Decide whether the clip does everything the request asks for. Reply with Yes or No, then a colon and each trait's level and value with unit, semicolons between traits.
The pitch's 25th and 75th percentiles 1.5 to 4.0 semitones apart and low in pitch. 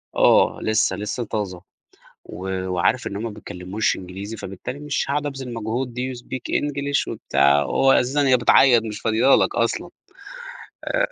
No: average, 5.2 semitones; low, 115 Hz